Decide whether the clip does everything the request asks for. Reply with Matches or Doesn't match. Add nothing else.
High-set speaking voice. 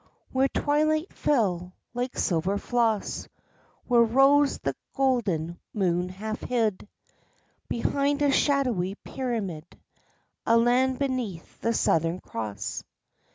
Matches